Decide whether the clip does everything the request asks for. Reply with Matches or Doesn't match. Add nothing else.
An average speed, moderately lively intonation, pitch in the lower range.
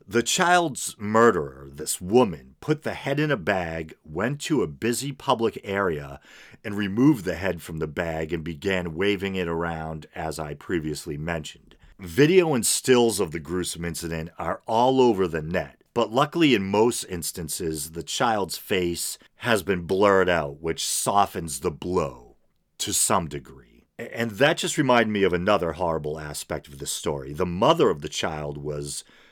Doesn't match